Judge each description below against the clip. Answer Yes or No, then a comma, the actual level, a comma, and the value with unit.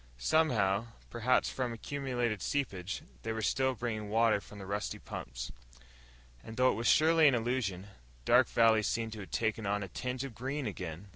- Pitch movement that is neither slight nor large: Yes, average, 3.9 semitones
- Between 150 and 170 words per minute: No, average, 180 wpm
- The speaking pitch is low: Yes, low, 115 Hz